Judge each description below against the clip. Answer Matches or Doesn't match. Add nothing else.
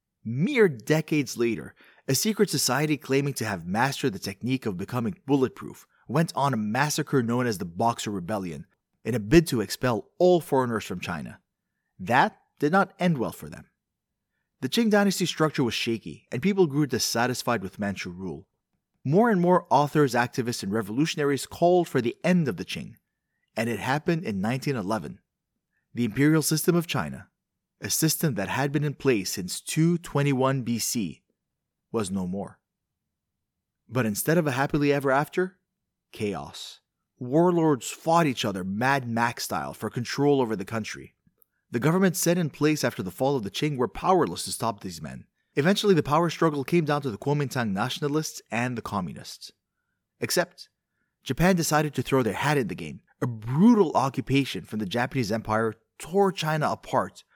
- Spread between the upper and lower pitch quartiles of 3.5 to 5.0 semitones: Doesn't match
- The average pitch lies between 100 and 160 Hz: Matches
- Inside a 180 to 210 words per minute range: Doesn't match